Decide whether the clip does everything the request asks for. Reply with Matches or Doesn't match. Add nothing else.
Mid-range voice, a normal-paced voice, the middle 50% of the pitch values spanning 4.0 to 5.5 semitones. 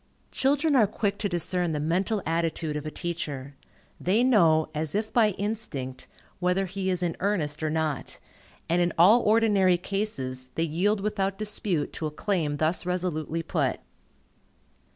Matches